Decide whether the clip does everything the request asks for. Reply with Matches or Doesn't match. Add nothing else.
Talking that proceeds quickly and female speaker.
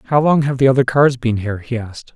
Doesn't match